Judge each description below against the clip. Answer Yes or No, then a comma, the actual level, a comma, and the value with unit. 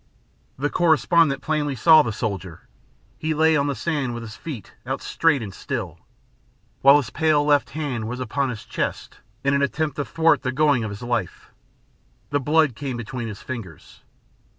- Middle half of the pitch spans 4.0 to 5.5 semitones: Yes, average, 4.5 semitones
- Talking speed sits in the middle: Yes, average, 175 wpm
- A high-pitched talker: No, medium, 140 Hz